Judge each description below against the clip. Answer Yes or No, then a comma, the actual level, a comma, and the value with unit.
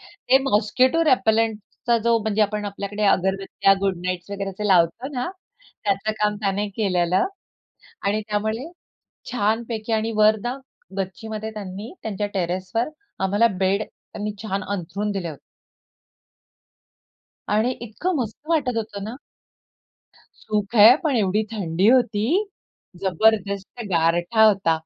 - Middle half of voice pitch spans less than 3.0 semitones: Yes, narrow, 2.4 semitones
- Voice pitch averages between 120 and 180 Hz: No, high, 210 Hz